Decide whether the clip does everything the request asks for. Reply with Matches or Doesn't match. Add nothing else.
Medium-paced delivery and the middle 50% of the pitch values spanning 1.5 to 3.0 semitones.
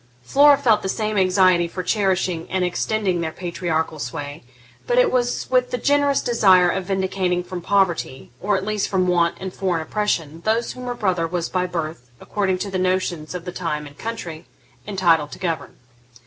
Doesn't match